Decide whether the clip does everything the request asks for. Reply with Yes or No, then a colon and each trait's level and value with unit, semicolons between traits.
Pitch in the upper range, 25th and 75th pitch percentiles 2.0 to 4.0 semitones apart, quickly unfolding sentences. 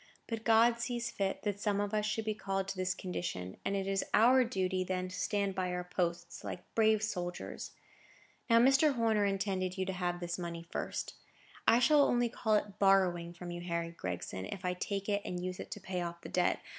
Yes: high, 195 Hz; average, 3.2 semitones; fast, 215 wpm